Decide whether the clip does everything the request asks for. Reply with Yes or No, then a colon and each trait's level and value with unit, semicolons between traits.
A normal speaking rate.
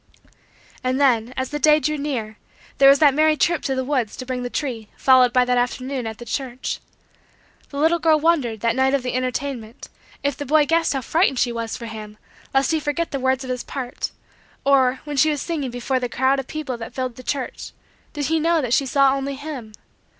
No: fast, 225 wpm